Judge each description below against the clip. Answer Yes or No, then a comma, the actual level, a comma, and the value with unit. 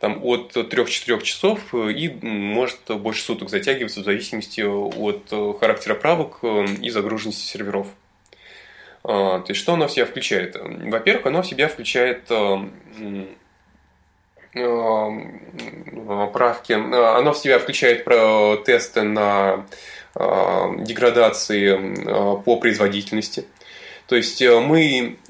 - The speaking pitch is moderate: No, low, 105 Hz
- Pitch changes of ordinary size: Yes, average, 3.0 semitones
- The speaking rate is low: Yes, slow, 95 wpm